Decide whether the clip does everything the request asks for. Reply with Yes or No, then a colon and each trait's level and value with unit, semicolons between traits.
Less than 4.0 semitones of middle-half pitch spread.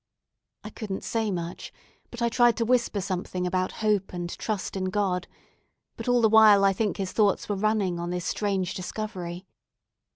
Yes: average, 2.9 semitones